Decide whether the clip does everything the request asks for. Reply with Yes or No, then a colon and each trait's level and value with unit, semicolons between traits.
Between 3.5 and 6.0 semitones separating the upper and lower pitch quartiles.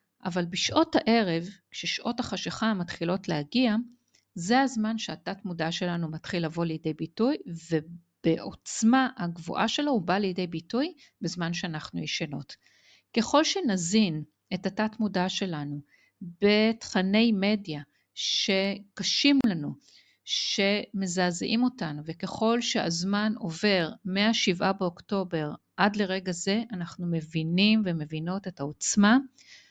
Yes: average, 4.6 semitones